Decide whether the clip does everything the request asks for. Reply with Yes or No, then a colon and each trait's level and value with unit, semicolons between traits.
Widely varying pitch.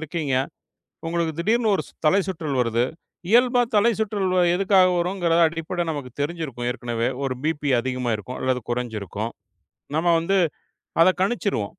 Yes: wide, 6.9 semitones